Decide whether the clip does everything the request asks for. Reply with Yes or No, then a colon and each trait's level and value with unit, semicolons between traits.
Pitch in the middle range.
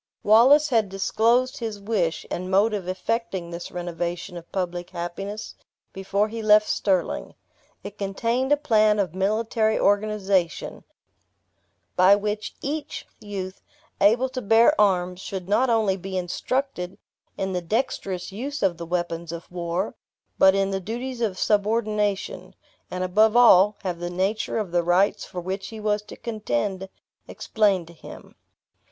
No: high, 200 Hz